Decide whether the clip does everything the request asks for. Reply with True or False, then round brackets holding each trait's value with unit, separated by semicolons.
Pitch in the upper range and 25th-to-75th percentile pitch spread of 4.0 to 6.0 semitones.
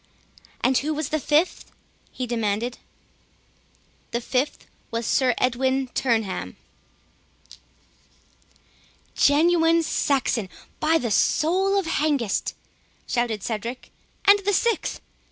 True (265 Hz; 5.4 semitones)